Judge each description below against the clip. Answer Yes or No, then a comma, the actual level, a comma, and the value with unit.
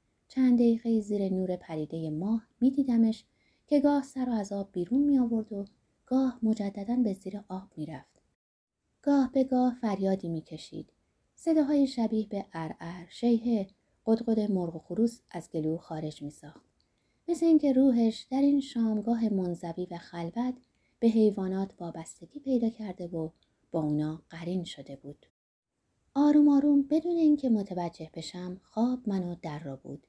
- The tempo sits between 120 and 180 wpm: Yes, fast, 155 wpm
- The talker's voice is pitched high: Yes, high, 210 Hz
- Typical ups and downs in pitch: No, wide, 6.5 semitones